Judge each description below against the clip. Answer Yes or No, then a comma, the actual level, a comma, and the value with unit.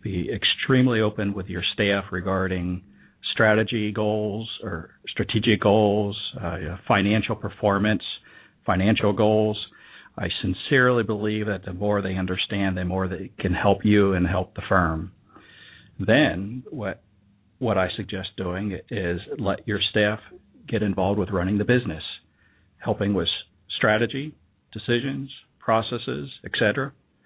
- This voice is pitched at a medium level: No, low, 105 Hz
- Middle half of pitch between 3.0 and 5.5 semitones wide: No, narrow, 2.5 semitones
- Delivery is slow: Yes, slow, 125 wpm